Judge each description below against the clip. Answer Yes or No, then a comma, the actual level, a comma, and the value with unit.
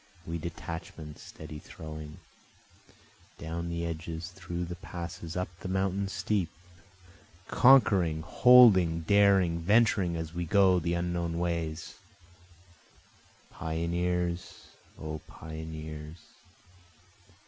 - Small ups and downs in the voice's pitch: Yes, narrow, 2.2 semitones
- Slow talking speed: Yes, slow, 95 wpm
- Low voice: Yes, very low, 85 Hz